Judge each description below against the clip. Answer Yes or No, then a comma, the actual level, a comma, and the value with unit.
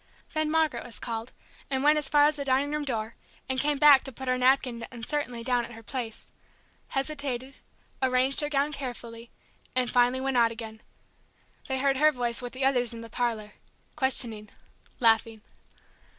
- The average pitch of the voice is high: Yes, very high, 255 Hz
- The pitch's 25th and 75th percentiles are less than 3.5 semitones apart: Yes, average, 3.0 semitones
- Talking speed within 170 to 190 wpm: Yes, average, 175 wpm